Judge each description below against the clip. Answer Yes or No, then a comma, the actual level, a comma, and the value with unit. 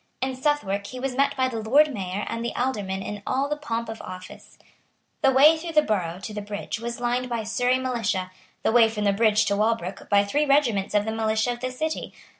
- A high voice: Yes, high, 230 Hz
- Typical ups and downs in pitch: Yes, average, 3.9 semitones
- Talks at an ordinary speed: No, fast, 230 wpm